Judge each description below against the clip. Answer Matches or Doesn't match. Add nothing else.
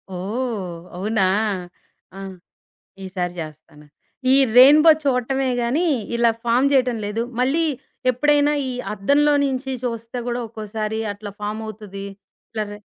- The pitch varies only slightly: Doesn't match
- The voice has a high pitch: Matches